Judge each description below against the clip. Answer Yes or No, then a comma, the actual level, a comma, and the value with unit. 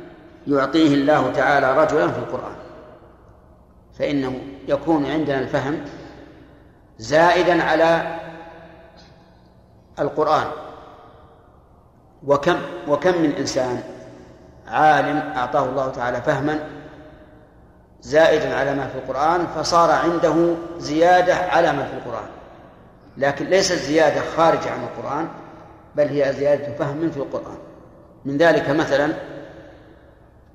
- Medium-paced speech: Yes, average, 95 wpm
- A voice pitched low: No, medium, 150 Hz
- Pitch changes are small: No, average, 3.2 semitones